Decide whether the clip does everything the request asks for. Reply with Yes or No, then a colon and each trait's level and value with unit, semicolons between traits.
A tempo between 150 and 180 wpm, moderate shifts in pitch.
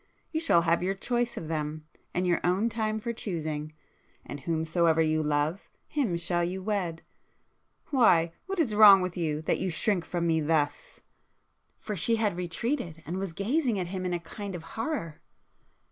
Yes: average, 170 wpm; average, 4.7 semitones